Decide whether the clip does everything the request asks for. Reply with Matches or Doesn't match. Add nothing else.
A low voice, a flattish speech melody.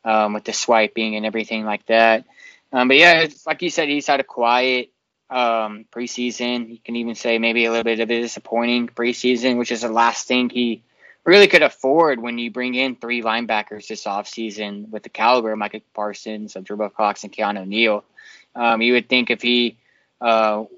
Matches